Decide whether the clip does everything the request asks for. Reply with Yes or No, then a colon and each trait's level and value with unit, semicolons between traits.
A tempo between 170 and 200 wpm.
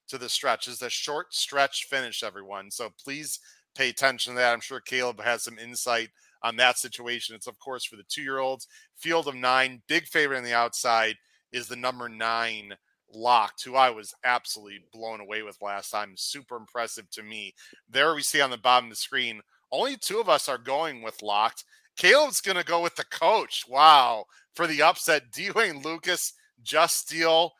Yes: average, 195 wpm